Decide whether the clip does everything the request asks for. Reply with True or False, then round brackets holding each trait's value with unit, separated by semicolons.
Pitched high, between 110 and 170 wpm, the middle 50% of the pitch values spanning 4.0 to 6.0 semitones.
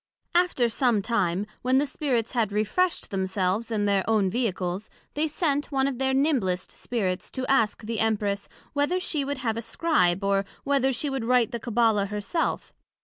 False (230 Hz; 180 wpm; 5.1 semitones)